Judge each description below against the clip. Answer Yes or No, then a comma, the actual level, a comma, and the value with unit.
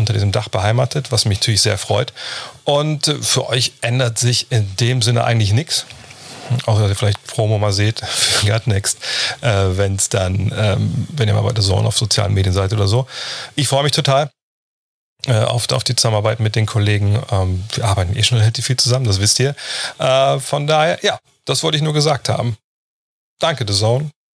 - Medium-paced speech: No, fast, 195 wpm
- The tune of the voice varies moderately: Yes, average, 3.6 semitones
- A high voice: No, low, 115 Hz